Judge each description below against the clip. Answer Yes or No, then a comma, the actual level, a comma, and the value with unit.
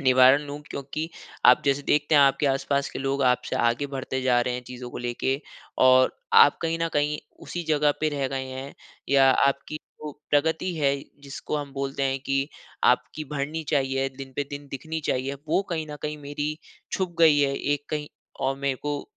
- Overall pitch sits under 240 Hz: Yes, medium, 140 Hz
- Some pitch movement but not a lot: No, narrow, 1.9 semitones